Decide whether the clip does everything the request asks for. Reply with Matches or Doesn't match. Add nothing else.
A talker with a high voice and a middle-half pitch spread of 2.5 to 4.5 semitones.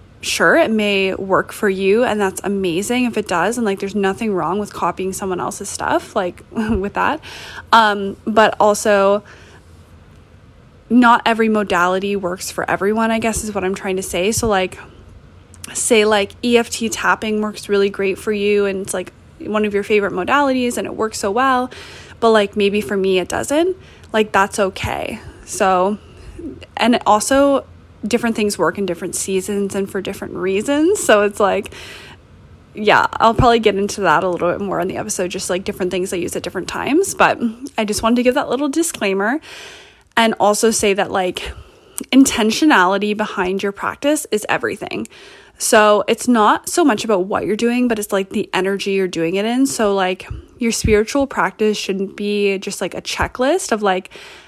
Matches